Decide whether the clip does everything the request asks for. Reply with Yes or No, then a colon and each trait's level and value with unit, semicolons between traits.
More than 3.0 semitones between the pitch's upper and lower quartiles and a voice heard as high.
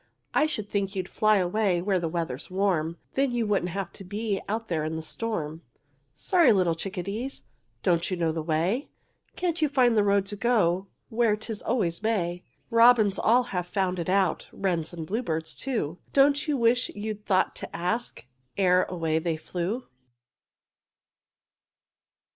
Yes: average, 4.7 semitones; high, 195 Hz